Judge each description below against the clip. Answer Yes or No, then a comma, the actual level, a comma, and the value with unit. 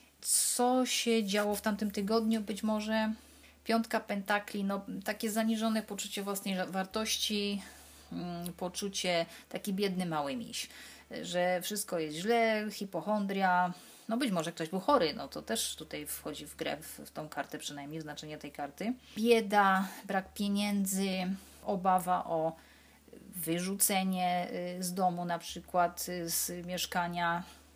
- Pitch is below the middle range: No, high, 195 Hz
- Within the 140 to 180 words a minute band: No, average, 130 wpm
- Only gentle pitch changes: No, average, 3.5 semitones